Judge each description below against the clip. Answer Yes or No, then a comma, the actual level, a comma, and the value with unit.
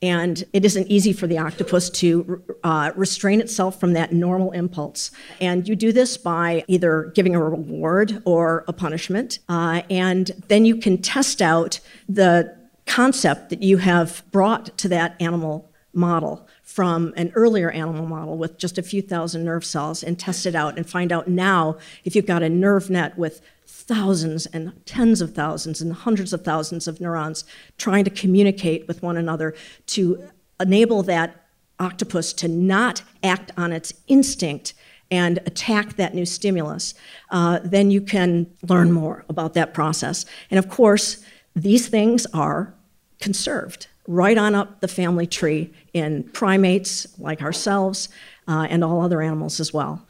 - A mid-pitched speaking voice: Yes, medium, 180 Hz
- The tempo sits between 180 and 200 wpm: No, average, 165 wpm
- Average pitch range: Yes, average, 3.0 semitones